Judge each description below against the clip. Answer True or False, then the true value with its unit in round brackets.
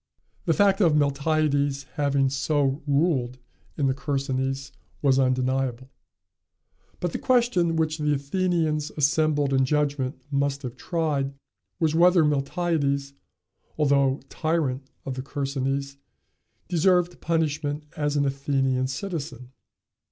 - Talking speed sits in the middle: False (115 wpm)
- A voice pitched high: False (145 Hz)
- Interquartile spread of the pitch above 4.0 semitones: False (2.6 semitones)